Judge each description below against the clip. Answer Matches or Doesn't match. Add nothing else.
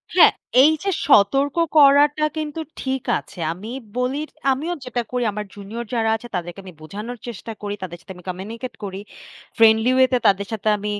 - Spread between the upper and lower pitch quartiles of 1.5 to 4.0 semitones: Doesn't match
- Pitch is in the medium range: Doesn't match